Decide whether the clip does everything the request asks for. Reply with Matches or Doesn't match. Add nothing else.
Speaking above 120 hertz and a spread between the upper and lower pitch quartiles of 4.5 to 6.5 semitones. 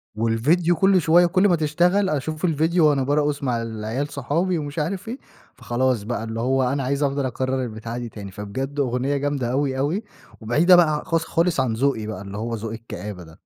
Matches